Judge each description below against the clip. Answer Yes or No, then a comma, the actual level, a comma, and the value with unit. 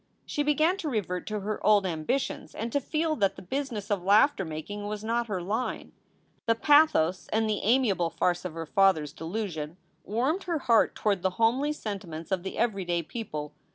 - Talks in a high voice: Yes, high, 210 Hz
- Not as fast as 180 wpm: No, average, 190 wpm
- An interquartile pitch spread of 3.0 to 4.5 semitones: No, average, 5.2 semitones